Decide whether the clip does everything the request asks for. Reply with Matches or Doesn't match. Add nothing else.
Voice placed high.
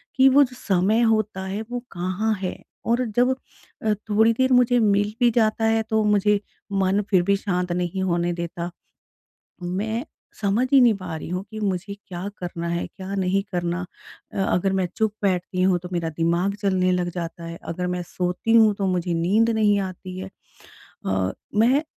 Matches